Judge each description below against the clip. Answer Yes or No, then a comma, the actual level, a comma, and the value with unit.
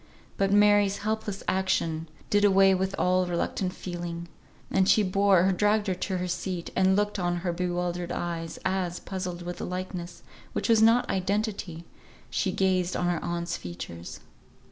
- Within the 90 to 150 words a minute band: No, average, 165 wpm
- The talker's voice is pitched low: No, medium, 185 Hz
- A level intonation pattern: Yes, narrow, 2.0 semitones